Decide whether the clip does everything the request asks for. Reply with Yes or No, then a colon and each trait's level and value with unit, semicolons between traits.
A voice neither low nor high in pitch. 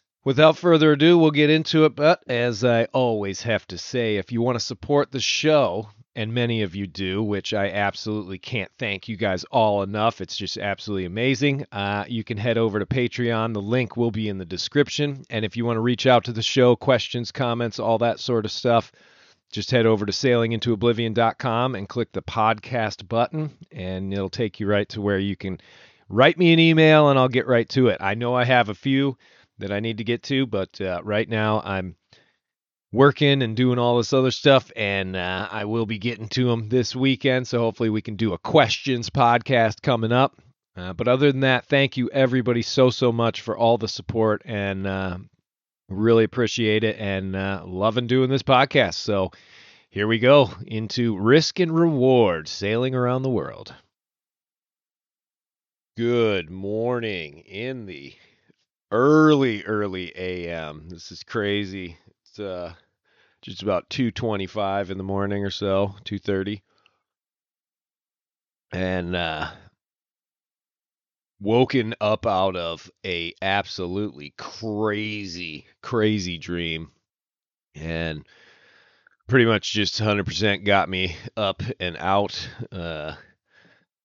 No: low, 110 Hz